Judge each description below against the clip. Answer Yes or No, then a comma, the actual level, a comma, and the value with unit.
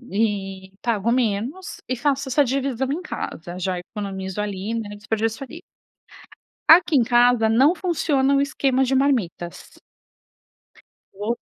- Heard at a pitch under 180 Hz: No, high, 235 Hz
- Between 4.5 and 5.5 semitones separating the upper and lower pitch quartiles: Yes, average, 5.0 semitones